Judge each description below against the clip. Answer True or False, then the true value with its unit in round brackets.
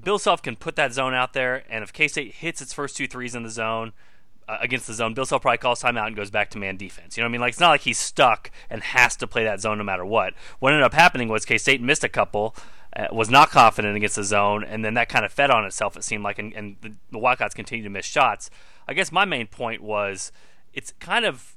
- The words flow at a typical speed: False (280 wpm)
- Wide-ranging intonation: False (3.4 semitones)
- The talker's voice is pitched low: True (115 Hz)